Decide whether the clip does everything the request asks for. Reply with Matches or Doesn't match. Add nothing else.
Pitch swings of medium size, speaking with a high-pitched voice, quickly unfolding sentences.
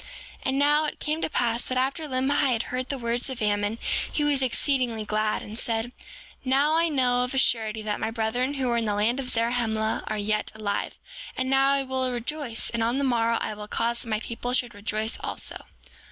Matches